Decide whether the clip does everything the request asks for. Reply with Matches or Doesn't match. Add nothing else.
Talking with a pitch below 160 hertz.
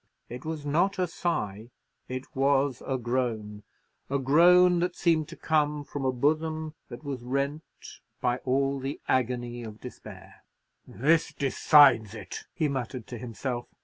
Matches